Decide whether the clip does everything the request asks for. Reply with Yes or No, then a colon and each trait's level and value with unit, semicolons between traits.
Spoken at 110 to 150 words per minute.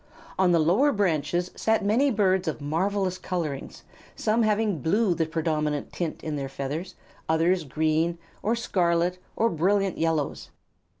Yes: average, 145 wpm